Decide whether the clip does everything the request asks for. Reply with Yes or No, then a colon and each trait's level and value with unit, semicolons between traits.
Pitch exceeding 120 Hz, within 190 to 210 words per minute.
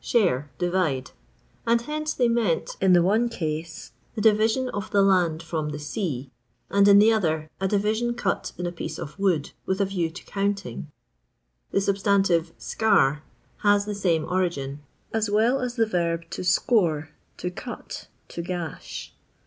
No: high, 190 Hz; average, 165 wpm